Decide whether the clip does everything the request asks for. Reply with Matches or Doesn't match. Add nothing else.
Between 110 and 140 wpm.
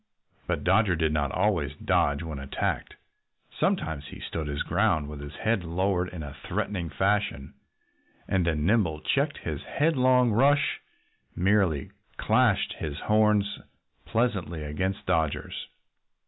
Matches